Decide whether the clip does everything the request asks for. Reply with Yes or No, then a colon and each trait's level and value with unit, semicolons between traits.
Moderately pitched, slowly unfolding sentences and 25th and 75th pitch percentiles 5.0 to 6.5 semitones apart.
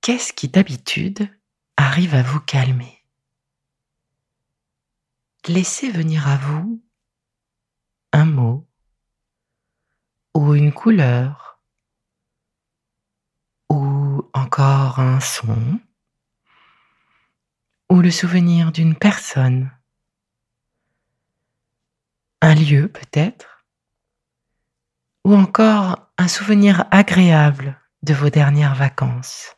Yes: medium, 145 Hz; slow, 75 wpm; wide, 5.4 semitones